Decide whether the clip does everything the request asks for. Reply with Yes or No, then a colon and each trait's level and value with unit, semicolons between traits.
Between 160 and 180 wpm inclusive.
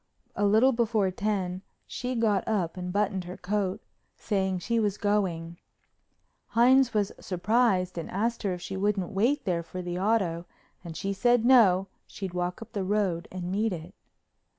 Yes: average, 170 wpm